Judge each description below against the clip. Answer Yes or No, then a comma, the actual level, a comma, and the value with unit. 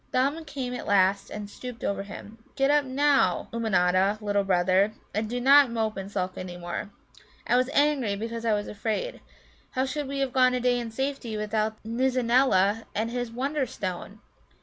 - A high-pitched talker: Yes, high, 230 Hz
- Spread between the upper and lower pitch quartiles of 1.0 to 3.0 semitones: No, average, 4.4 semitones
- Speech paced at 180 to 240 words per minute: Yes, average, 185 wpm